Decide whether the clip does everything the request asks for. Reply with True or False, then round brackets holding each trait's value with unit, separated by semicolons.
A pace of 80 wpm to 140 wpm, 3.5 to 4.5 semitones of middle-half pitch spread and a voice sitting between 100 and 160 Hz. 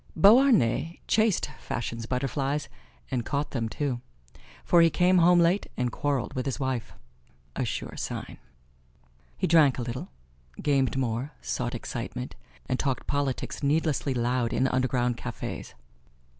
True (135 wpm; 3.9 semitones; 135 Hz)